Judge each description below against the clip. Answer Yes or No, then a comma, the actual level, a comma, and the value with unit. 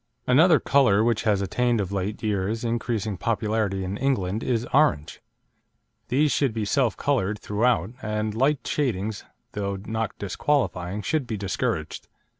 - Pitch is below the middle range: Yes, low, 110 Hz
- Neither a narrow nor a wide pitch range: Yes, average, 3.9 semitones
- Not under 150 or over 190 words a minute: No, average, 140 wpm